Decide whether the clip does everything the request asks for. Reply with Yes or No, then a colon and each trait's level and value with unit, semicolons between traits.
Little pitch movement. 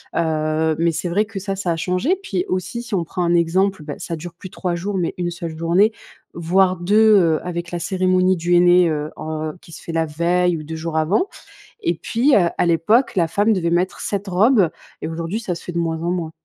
Yes: narrow, 2.3 semitones